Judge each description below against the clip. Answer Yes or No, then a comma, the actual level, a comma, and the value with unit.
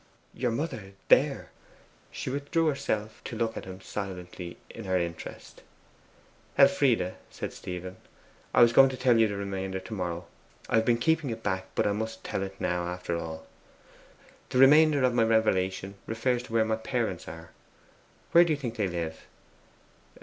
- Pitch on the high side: No, low, 110 Hz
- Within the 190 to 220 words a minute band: No, average, 170 wpm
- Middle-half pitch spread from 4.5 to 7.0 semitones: Yes, average, 5.1 semitones